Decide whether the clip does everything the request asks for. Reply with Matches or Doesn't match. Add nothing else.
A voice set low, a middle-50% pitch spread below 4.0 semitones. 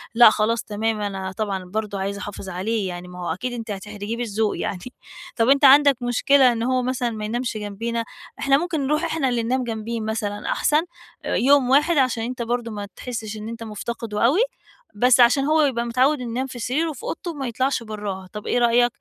Doesn't match